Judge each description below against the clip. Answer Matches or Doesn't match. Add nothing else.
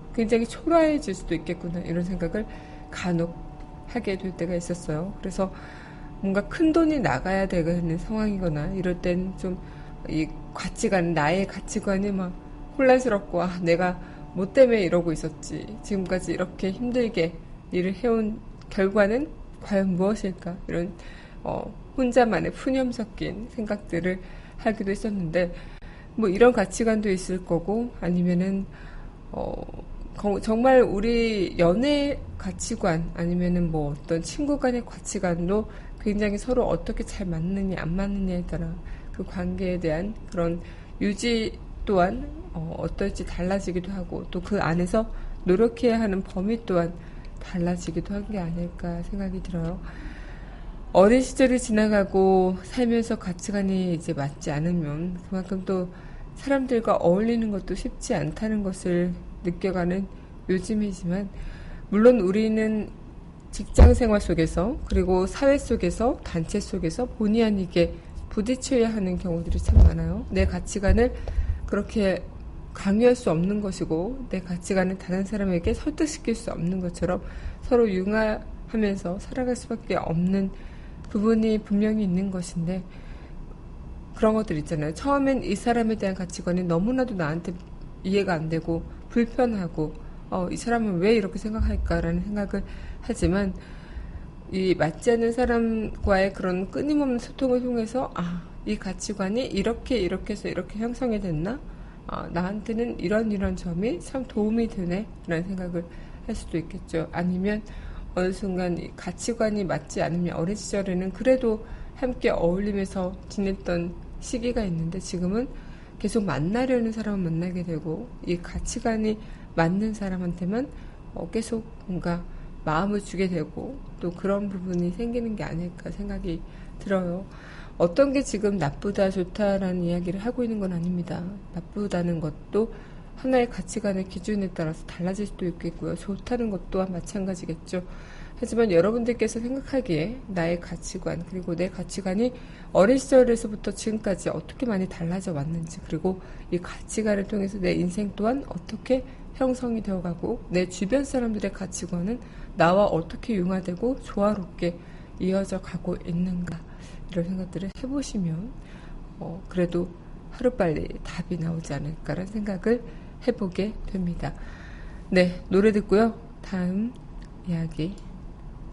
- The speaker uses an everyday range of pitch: Matches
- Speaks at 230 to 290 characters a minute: Doesn't match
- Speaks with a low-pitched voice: Doesn't match